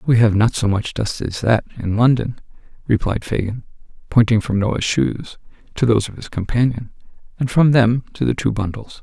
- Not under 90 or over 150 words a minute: No, average, 185 wpm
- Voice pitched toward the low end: Yes, low, 110 Hz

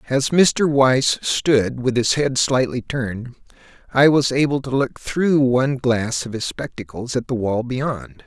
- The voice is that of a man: Yes, male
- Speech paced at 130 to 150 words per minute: No, average, 175 wpm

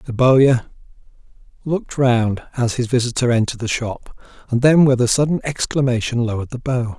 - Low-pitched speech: Yes, low, 125 Hz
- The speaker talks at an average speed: Yes, average, 165 wpm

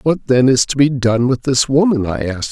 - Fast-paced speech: Yes, fast, 265 wpm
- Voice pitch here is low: Yes, low, 130 Hz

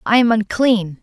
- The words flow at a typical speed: Yes, average, 175 wpm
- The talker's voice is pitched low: No, high, 215 Hz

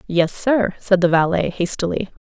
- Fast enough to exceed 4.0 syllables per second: Yes, 4.6 syllables/s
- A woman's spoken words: Yes, female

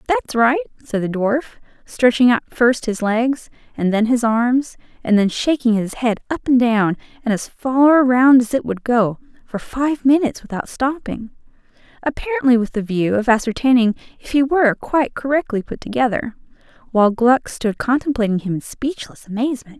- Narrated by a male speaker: No, female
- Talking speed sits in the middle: Yes, average, 170 wpm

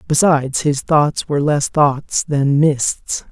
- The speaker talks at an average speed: Yes, average, 145 wpm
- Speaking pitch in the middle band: Yes, medium, 145 Hz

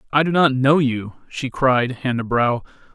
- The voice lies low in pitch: Yes, low, 130 Hz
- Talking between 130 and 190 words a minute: No, fast, 205 wpm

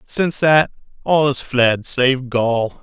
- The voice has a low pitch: Yes, low, 130 Hz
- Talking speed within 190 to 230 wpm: No, average, 150 wpm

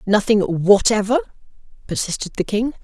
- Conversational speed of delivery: No, slow, 105 wpm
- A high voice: Yes, high, 215 Hz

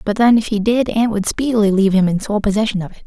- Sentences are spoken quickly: Yes, fast, 295 wpm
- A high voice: Yes, high, 210 Hz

